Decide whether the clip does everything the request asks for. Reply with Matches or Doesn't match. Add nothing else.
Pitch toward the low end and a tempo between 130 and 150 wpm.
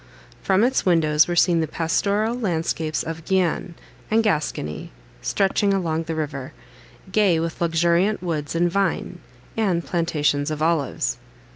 Doesn't match